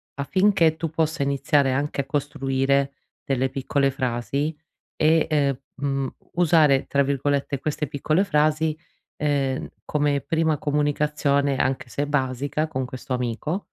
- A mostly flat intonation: Yes, narrow, 2.1 semitones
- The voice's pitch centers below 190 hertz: Yes, medium, 140 Hz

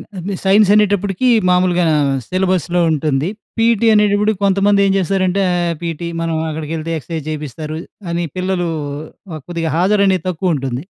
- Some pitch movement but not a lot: Yes, average, 3.5 semitones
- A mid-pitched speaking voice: Yes, medium, 180 Hz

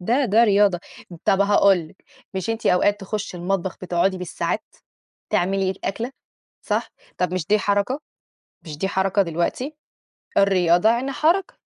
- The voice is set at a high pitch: Yes, high, 195 Hz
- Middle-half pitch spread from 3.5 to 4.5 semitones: No, average, 3.1 semitones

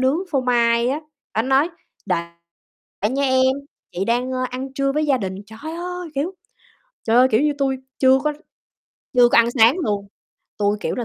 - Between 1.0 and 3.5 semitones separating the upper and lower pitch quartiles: Yes, average, 2.9 semitones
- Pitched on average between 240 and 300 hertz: Yes, very high, 260 Hz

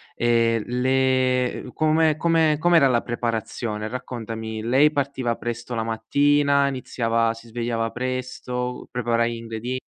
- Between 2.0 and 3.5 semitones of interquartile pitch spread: Yes, narrow, 2.5 semitones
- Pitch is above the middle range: No, low, 125 Hz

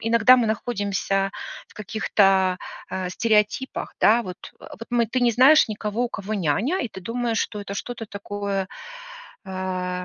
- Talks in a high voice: Yes, high, 210 Hz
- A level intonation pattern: No, average, 3.3 semitones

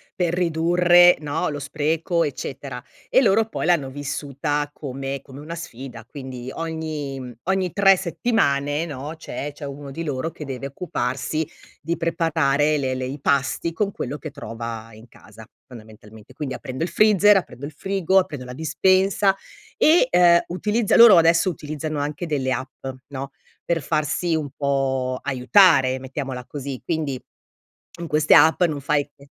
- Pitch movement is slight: No, average, 4.0 semitones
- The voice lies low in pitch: No, medium, 145 Hz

